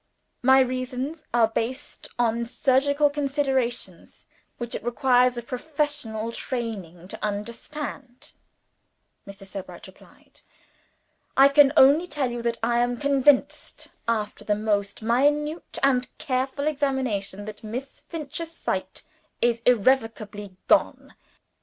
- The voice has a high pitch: Yes, very high, 250 Hz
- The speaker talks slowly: Yes, slow, 115 wpm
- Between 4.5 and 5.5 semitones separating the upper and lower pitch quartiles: No, average, 3.8 semitones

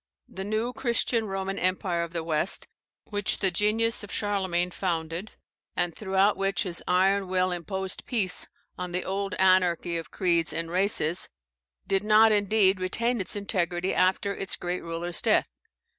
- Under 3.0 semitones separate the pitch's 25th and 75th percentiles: Yes, narrow, 2.5 semitones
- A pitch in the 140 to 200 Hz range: Yes, high, 190 Hz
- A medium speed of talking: Yes, average, 155 wpm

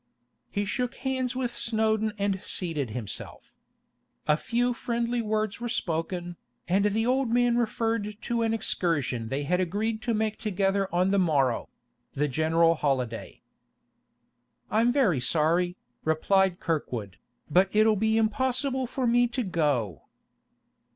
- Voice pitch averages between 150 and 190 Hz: No, high, 205 Hz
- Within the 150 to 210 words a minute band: No, slow, 135 wpm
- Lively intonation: Yes, wide, 6.0 semitones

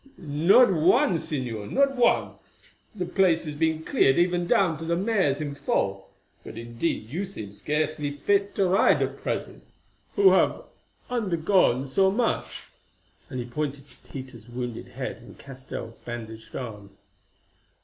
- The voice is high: No, medium, 150 Hz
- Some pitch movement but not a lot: No, wide, 7.2 semitones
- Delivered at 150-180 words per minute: No, average, 140 wpm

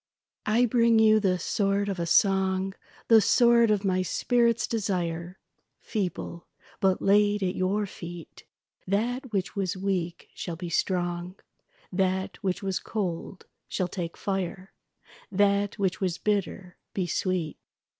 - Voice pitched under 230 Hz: Yes, high, 190 Hz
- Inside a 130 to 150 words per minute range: Yes, slow, 135 wpm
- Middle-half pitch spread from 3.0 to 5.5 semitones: No, narrow, 2.4 semitones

